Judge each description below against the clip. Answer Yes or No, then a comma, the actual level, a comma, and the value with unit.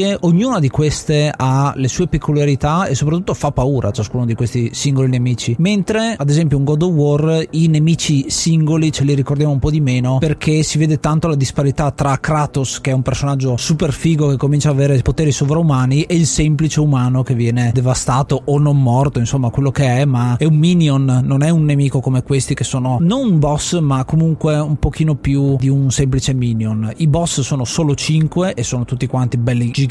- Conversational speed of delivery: No, fast, 205 wpm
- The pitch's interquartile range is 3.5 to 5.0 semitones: No, average, 2.9 semitones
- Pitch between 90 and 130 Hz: No, medium, 140 Hz